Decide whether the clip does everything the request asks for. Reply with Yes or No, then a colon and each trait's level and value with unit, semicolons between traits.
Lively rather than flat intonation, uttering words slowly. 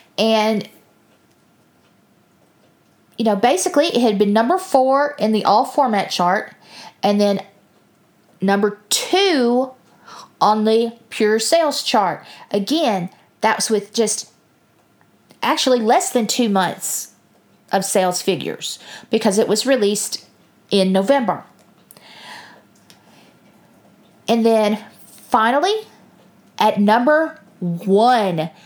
No: average, 4.2 semitones; slow, 100 wpm